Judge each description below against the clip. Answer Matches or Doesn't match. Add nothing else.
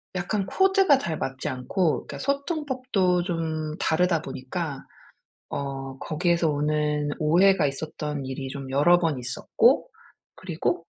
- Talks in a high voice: Doesn't match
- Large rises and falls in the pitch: Doesn't match